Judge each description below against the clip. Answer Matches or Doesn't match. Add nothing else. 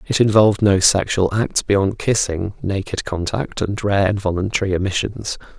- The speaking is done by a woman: Doesn't match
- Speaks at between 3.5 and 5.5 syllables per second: Matches